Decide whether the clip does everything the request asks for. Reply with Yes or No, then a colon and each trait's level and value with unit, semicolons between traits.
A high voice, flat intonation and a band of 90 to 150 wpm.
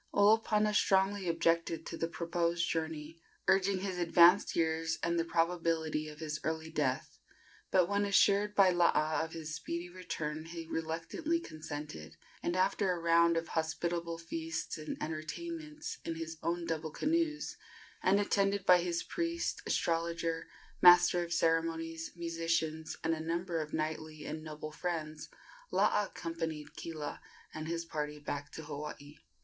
No: medium, 165 Hz; narrow, 2.0 semitones; average, 145 wpm